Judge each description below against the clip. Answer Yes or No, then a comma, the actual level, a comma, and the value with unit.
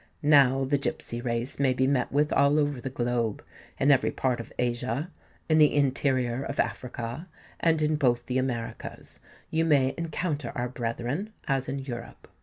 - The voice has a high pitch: No, low, 135 Hz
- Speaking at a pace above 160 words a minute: Yes, average, 170 wpm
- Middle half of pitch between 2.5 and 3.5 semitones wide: Yes, average, 3.1 semitones